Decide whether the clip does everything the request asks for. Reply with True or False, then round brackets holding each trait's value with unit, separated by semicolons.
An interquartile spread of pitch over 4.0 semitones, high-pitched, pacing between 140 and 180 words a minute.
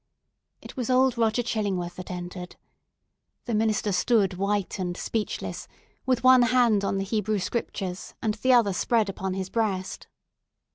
False (3.7 semitones; 210 Hz; 150 wpm)